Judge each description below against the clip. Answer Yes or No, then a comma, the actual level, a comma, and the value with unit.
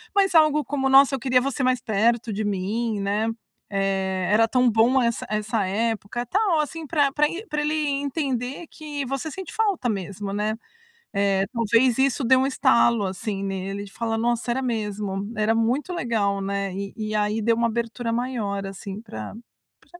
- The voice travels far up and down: No, average, 4.8 semitones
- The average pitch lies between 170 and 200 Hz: No, high, 230 Hz